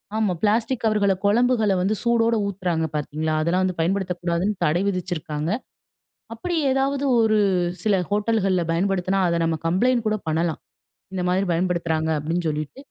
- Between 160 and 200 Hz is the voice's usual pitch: Yes, medium, 185 Hz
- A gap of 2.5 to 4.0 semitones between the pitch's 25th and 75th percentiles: No, average, 4.4 semitones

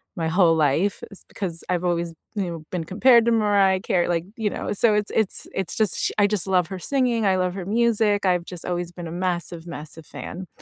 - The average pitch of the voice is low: No, medium, 185 Hz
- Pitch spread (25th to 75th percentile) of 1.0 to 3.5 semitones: Yes, average, 3.2 semitones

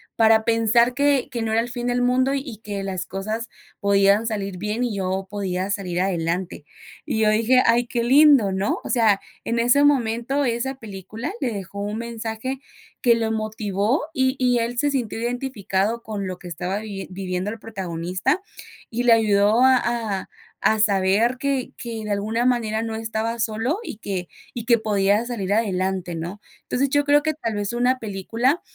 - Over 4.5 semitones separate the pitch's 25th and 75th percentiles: No, average, 3.5 semitones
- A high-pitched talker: Yes, high, 220 Hz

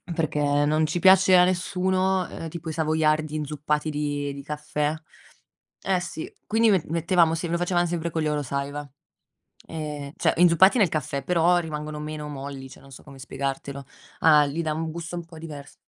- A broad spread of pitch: No, average, 2.7 semitones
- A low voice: No, medium, 155 Hz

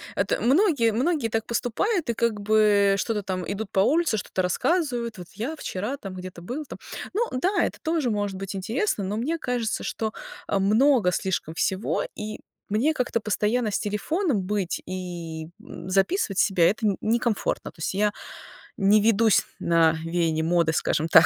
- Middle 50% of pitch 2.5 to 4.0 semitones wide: No, average, 4.5 semitones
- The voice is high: Yes, high, 210 Hz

